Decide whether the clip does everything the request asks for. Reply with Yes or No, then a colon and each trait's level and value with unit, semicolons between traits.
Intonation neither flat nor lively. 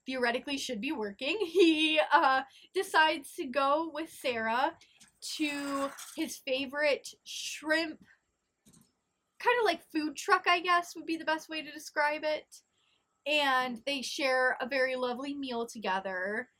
Yes: average, 3.5 semitones